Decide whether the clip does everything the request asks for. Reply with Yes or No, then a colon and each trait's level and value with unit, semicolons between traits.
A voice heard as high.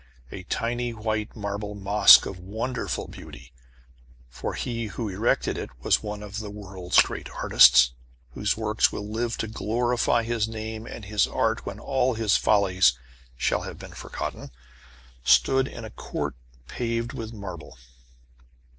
No: low, 105 Hz